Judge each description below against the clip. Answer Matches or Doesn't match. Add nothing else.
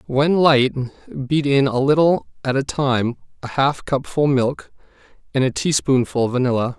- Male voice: Matches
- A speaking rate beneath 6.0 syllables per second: Matches